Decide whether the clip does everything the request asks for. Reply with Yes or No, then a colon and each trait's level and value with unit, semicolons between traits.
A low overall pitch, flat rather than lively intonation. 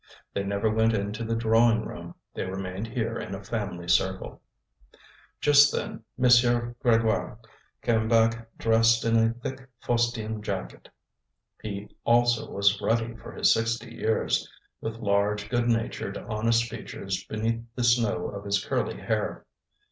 Yes: low, 115 Hz; narrow, 2.2 semitones